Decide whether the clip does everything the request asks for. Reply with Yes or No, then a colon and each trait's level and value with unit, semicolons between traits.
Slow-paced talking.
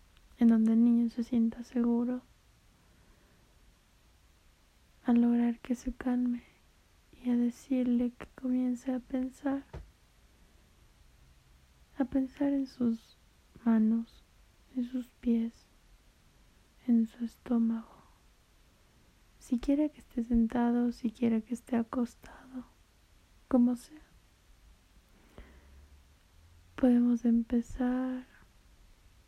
Yes: slow, 85 wpm